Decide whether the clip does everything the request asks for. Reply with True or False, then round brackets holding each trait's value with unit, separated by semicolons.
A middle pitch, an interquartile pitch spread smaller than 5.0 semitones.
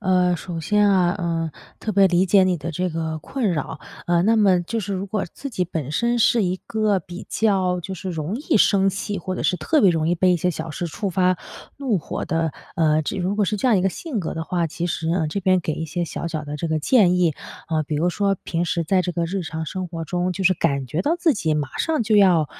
True (180 Hz; 3.3 semitones)